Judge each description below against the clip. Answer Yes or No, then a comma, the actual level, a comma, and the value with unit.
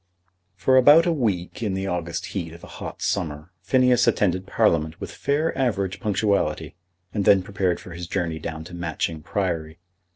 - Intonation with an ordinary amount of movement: Yes, average, 4.3 semitones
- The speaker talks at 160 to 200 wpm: Yes, average, 170 wpm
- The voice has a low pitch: Yes, very low, 95 Hz